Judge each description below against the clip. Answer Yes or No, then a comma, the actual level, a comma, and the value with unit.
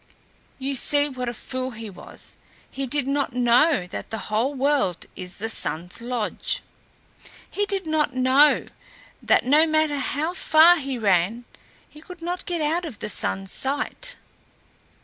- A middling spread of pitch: Yes, average, 5.0 semitones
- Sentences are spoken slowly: No, average, 155 wpm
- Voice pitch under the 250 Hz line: No, very high, 270 Hz